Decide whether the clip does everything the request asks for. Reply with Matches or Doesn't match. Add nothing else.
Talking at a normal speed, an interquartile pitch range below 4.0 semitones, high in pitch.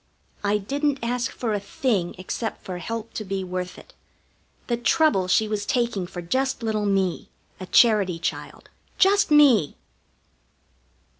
Doesn't match